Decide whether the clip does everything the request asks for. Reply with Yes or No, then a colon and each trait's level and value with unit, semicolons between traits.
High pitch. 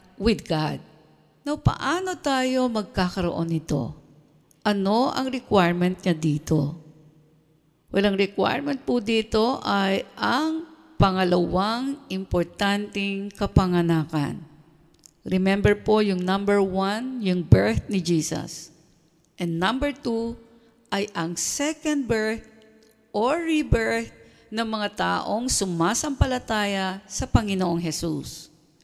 Yes: high, 195 Hz